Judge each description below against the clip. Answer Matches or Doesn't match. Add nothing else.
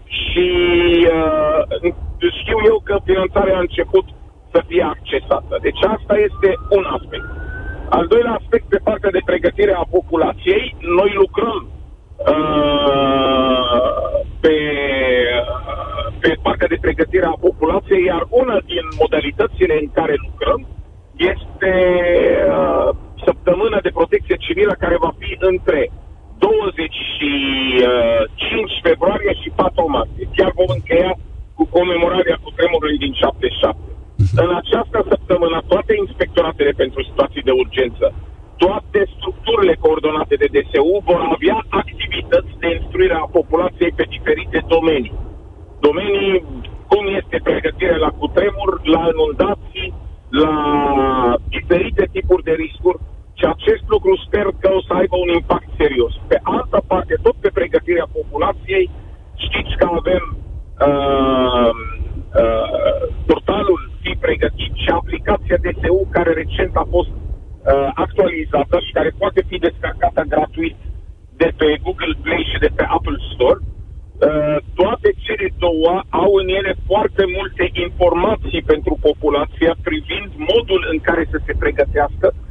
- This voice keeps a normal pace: Matches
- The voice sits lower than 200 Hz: Matches